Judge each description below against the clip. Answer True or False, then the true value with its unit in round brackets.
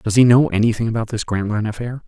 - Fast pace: True (230 wpm)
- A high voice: False (110 Hz)